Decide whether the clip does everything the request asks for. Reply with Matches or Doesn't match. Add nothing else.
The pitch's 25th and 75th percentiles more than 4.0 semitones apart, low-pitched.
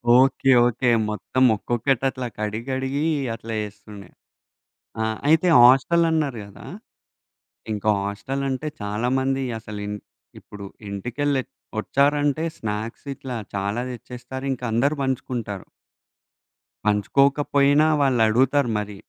Matches